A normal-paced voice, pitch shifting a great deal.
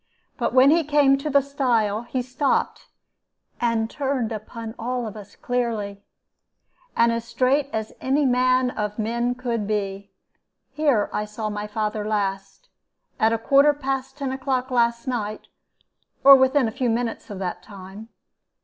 No: average, 155 wpm; average, 3.6 semitones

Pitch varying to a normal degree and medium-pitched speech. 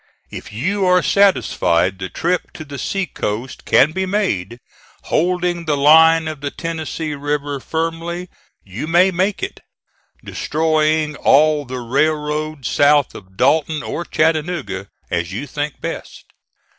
Yes: average, 3.2 semitones; medium, 155 Hz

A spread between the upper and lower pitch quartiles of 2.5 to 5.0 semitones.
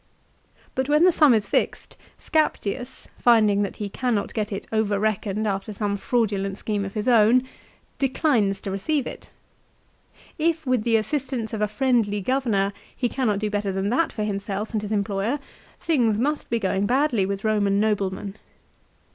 Yes: average, 3.8 semitones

